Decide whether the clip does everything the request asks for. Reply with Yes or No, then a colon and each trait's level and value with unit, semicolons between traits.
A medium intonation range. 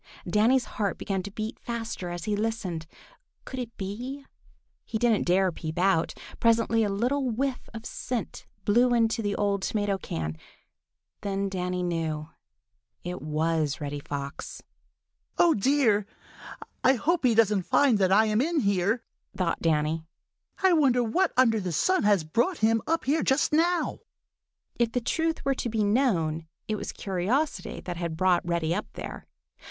No: wide, 5.7 semitones